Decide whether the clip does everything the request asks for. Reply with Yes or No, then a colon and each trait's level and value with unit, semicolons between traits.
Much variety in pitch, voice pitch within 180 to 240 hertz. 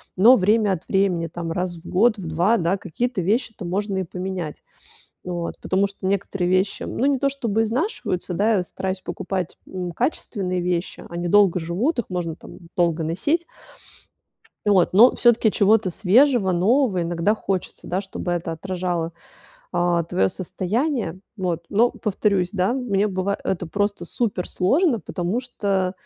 No: average, 3.6 semitones; high, 190 Hz